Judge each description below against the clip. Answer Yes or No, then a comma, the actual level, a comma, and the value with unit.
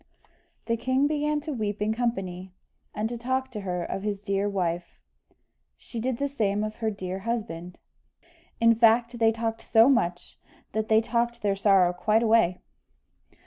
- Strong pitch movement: No, average, 3.3 semitones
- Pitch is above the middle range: Yes, high, 220 Hz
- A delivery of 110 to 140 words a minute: No, average, 165 wpm